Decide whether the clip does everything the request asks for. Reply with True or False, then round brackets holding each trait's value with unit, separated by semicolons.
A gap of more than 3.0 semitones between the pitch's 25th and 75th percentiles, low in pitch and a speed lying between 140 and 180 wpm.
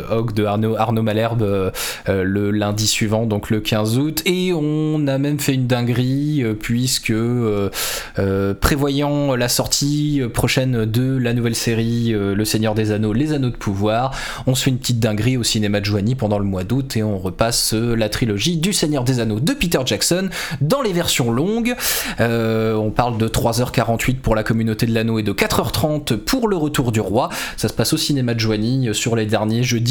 False (3.8 semitones; 115 Hz; 200 wpm)